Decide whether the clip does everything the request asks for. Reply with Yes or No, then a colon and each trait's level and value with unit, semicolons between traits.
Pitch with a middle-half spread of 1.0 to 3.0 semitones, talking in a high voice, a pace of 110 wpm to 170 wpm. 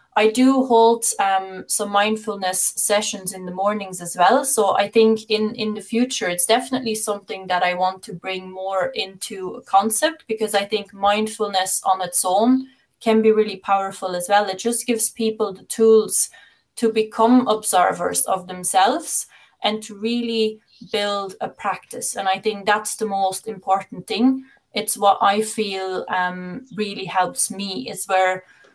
Yes: average, 2.7 semitones; high, 210 Hz; average, 165 wpm